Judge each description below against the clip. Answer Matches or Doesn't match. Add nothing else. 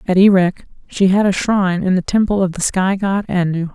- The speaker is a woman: Matches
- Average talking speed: Doesn't match